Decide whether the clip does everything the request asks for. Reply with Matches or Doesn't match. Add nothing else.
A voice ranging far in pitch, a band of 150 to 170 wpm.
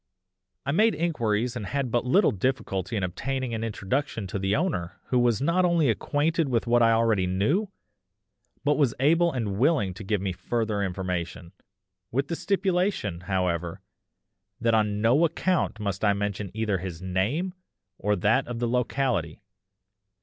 Matches